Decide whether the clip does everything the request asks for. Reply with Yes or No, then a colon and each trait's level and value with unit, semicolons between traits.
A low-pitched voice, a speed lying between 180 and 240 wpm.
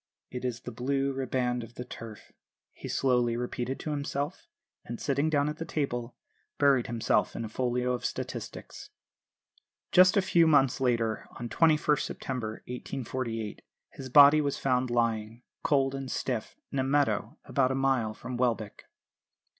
No: low, 130 Hz; average, 155 wpm